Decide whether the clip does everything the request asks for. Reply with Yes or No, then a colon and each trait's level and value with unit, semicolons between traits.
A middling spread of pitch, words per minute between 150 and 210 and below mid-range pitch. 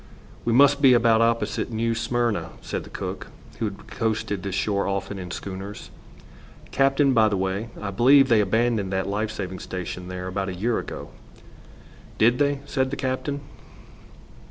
Yes: average, 3.9 semitones; average, 165 wpm; low, 110 Hz